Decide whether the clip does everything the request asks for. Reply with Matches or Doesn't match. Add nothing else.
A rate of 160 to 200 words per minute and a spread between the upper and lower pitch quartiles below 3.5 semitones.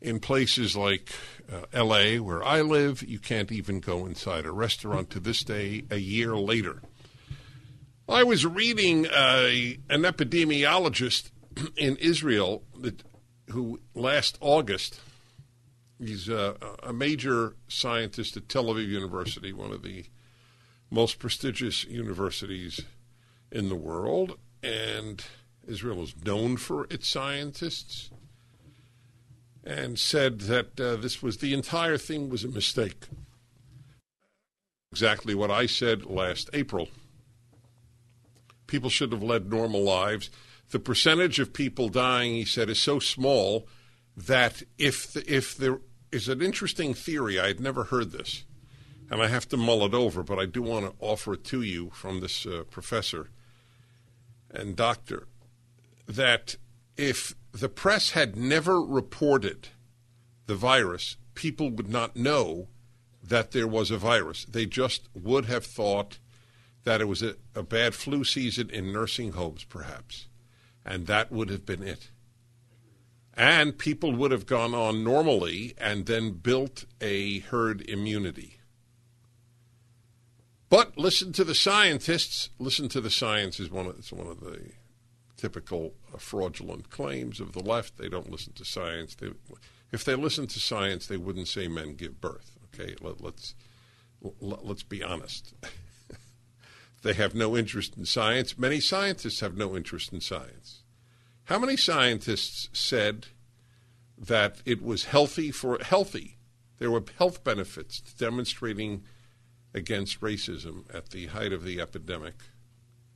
Doesn't match